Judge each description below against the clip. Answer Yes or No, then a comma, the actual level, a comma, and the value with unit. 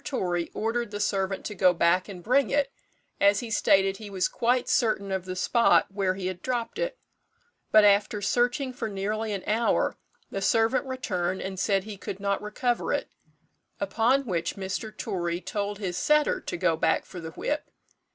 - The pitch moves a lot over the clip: No, average, 3.8 semitones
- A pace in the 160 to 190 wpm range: Yes, average, 180 wpm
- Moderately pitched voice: No, high, 205 Hz